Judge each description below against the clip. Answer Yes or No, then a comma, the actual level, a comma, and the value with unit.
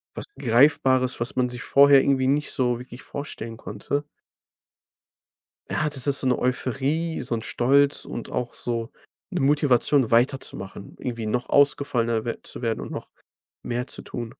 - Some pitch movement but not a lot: Yes, average, 3.0 semitones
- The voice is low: Yes, low, 125 Hz